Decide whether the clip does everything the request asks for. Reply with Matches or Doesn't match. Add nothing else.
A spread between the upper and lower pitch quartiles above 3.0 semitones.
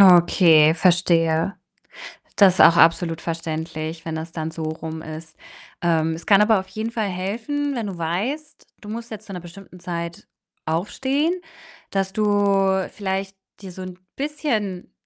Matches